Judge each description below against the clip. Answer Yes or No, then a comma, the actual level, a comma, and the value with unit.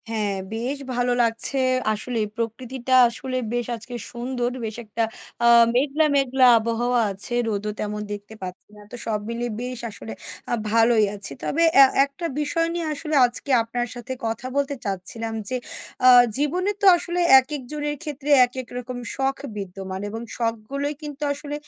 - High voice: Yes, high, 245 Hz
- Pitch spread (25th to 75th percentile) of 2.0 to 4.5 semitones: Yes, average, 3.7 semitones